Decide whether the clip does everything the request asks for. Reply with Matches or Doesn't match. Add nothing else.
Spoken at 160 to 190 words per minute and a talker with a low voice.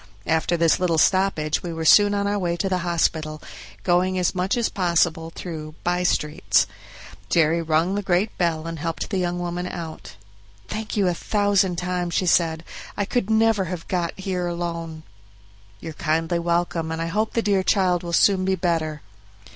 Doesn't match